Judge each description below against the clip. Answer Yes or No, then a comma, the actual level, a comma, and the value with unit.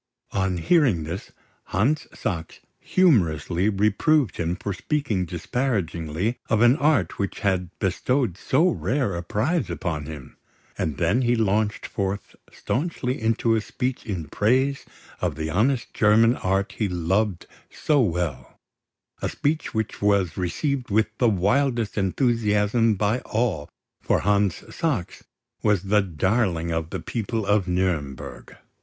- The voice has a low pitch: Yes, low, 105 Hz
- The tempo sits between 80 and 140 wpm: Yes, slow, 135 wpm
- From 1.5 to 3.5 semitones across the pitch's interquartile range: No, average, 5.2 semitones